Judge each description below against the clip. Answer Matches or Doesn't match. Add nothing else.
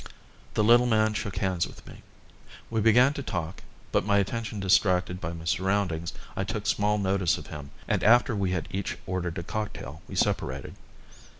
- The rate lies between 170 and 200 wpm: Matches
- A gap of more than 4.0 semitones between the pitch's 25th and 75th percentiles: Doesn't match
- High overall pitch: Doesn't match